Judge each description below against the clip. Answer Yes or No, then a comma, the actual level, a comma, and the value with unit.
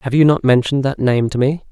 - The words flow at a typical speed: No, fast, 280 wpm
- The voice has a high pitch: No, low, 130 Hz